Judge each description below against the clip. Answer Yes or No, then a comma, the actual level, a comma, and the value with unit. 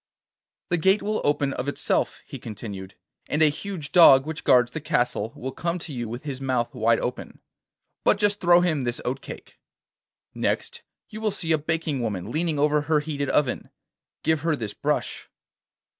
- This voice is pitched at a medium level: Yes, medium, 150 Hz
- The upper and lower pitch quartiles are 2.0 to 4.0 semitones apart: No, average, 4.9 semitones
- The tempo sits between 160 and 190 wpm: Yes, average, 180 wpm